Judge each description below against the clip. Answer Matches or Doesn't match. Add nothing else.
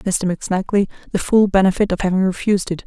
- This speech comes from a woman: Matches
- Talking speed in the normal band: Matches